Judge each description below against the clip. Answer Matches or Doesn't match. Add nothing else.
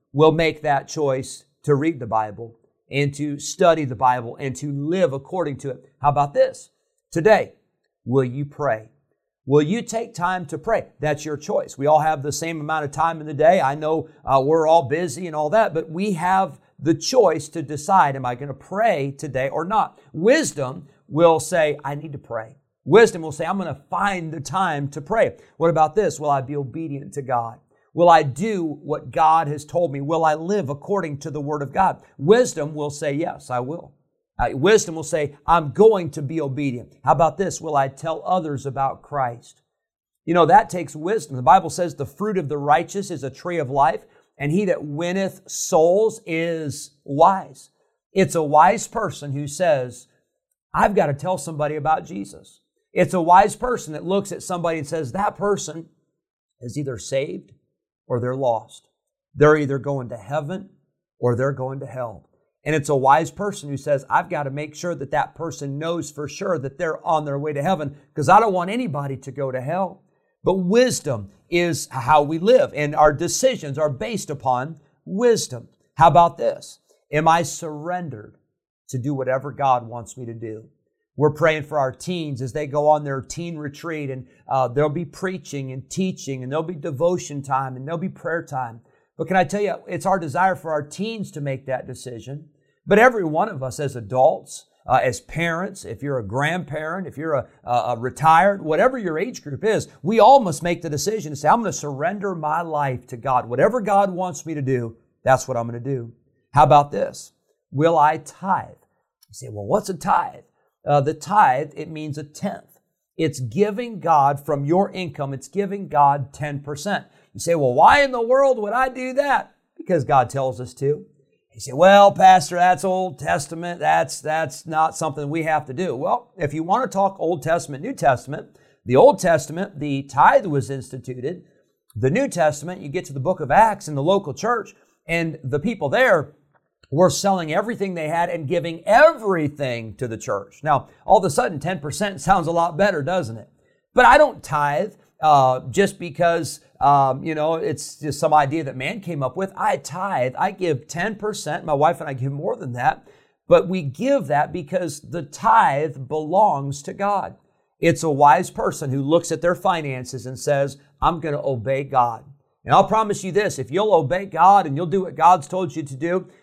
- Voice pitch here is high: Doesn't match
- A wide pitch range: Doesn't match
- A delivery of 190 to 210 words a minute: Matches